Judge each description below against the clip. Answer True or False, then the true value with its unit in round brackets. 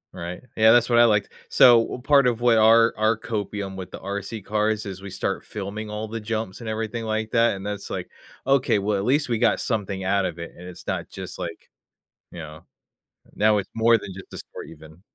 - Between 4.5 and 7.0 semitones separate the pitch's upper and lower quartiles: False (2.8 semitones)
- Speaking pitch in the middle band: False (110 Hz)